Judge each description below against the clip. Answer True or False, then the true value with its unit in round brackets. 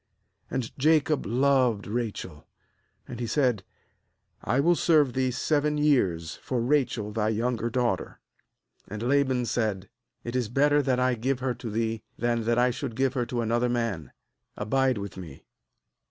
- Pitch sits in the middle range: False (120 Hz)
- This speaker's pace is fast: False (155 wpm)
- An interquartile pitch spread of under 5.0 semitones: True (3.2 semitones)